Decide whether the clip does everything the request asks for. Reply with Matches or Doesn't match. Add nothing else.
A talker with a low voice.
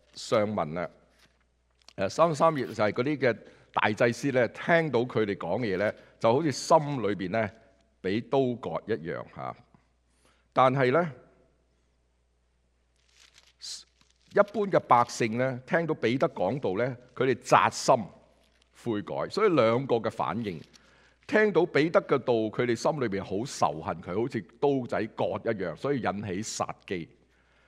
Matches